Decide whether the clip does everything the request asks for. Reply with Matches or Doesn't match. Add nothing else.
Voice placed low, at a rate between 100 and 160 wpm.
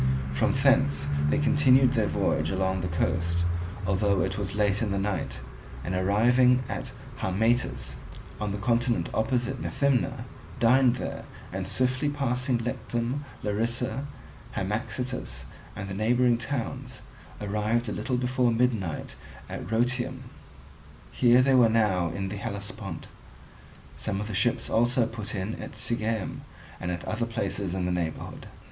Matches